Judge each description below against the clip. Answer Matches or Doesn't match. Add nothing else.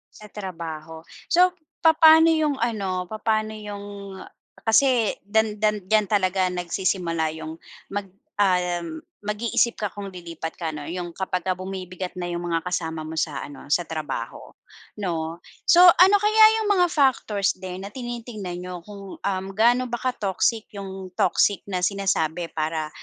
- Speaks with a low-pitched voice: Doesn't match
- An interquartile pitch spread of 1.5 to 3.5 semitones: Doesn't match